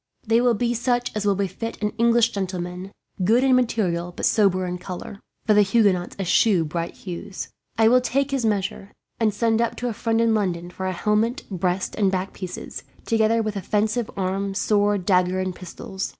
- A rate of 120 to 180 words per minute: No, average, 190 wpm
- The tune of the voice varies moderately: Yes, average, 3.6 semitones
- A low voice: No, high, 205 Hz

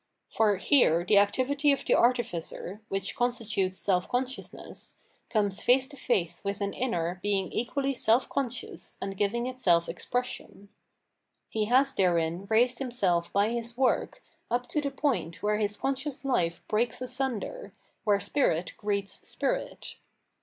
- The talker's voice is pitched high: Yes, high, 220 Hz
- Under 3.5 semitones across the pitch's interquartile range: No, average, 4.6 semitones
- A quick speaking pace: No, average, 145 wpm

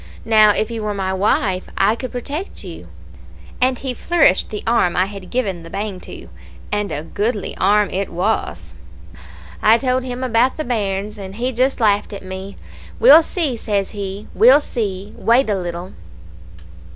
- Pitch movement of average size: Yes, average, 4.1 semitones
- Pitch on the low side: No, high, 210 Hz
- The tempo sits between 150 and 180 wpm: Yes, average, 170 wpm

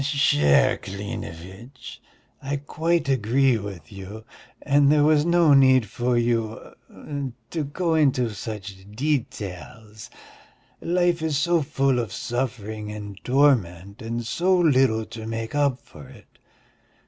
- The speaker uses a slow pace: Yes, slow, 125 wpm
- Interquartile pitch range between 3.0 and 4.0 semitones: No, average, 5.3 semitones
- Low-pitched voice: Yes, low, 125 Hz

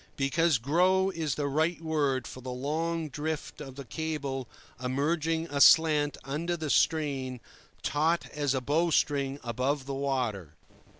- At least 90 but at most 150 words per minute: Yes, average, 140 wpm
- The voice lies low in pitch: No, medium, 145 Hz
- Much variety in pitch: No, average, 3.1 semitones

